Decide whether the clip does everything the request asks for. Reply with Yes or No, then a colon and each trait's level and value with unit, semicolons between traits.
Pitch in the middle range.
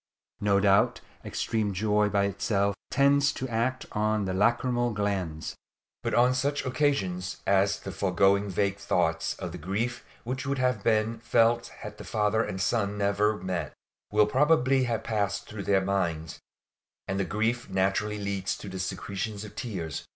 No: low, 105 Hz